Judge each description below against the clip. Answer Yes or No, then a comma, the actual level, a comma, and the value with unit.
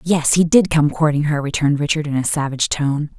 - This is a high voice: No, medium, 150 Hz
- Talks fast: Yes, fast, 225 wpm